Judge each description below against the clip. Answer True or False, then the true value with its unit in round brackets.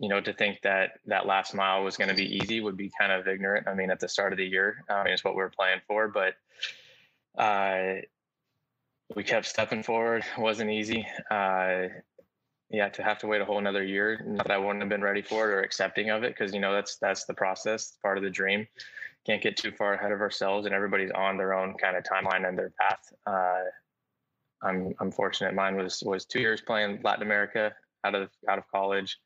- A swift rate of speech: True (230 wpm)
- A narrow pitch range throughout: True (1.5 semitones)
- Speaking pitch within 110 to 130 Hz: False (100 Hz)